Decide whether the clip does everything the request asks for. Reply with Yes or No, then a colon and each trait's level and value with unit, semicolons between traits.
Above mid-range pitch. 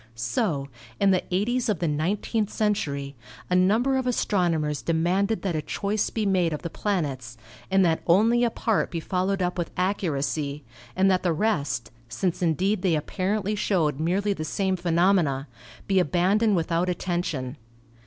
No: medium, 180 Hz